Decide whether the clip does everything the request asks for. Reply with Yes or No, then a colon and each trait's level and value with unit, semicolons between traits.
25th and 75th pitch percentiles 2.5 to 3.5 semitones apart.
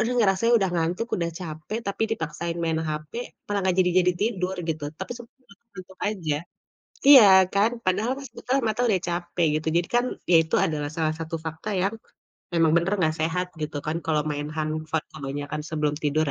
No: average, 4.2 semitones